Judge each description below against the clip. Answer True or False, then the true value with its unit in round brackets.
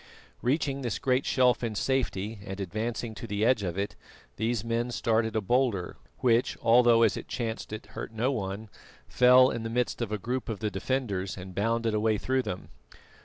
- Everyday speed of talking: True (190 wpm)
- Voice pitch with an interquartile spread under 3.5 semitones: True (3.1 semitones)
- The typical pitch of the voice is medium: False (115 Hz)